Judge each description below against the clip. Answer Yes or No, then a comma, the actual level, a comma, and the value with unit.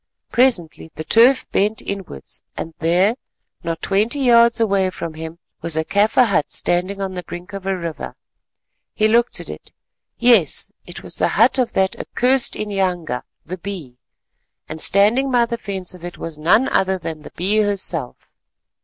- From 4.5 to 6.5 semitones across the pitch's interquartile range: Yes, average, 5.1 semitones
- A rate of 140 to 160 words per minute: No, average, 170 wpm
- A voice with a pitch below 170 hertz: No, high, 195 Hz